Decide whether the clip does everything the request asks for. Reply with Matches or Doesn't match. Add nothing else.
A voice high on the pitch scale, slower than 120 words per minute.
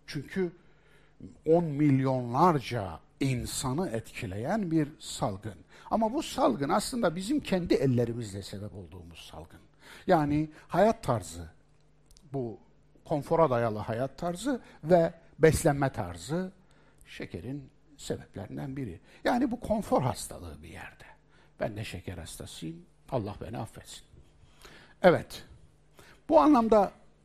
Doesn't match